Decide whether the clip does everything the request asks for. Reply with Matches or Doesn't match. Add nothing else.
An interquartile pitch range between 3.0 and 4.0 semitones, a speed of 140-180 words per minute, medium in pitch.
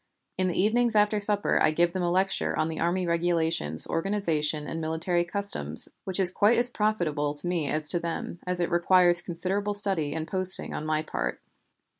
Doesn't match